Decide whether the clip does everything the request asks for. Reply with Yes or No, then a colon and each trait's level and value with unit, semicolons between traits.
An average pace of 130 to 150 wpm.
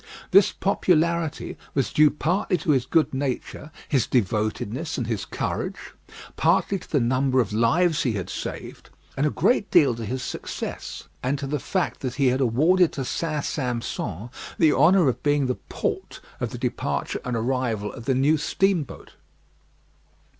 No: average, 165 wpm